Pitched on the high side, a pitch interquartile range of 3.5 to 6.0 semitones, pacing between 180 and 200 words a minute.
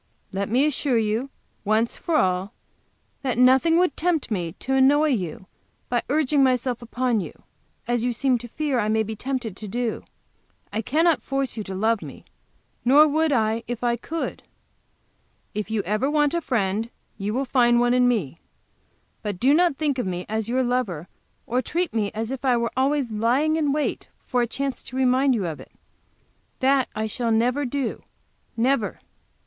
Yes: high, 245 Hz; average, 3.9 semitones; average, 185 wpm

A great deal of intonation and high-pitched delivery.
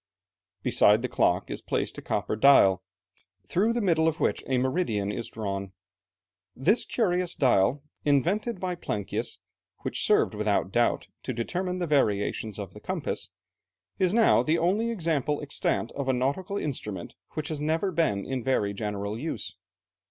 No: wide, 8.7 semitones; medium, 140 Hz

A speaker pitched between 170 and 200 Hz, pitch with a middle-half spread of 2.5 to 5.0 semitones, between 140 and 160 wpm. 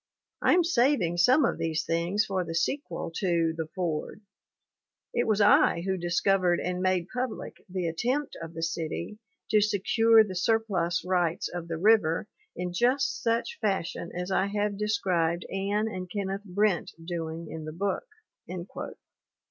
Yes: medium, 185 Hz; average, 3.8 semitones; average, 155 wpm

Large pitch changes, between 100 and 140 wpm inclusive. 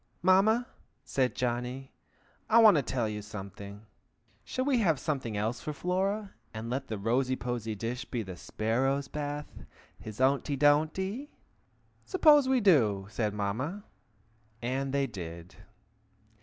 Yes: wide, 7.9 semitones; slow, 135 wpm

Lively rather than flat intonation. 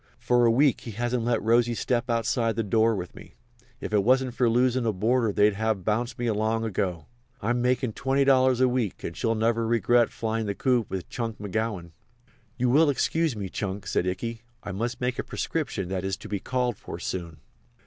No: average, 3.0 semitones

